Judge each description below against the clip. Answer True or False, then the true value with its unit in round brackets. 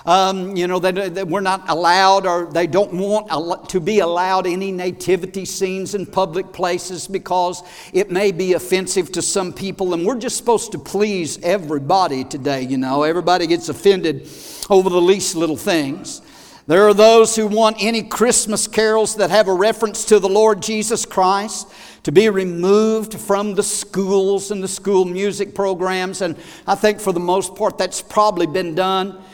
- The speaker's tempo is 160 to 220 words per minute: True (175 wpm)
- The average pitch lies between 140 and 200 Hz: True (190 Hz)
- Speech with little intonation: True (2.3 semitones)